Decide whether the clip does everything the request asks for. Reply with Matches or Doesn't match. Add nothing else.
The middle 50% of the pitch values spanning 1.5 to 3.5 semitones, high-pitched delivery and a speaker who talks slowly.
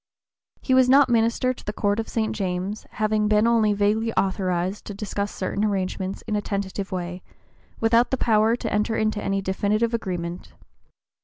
Doesn't match